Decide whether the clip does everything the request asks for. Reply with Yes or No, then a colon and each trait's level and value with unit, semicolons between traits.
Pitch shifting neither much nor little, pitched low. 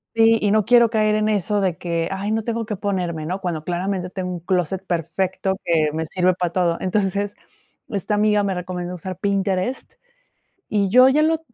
No: average, 3.0 semitones; high, 190 Hz